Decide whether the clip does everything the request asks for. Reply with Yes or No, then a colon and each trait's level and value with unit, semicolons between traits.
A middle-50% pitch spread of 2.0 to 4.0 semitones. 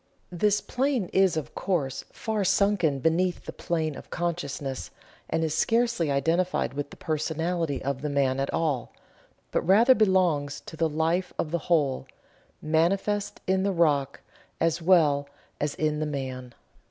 No: average, 4.4 semitones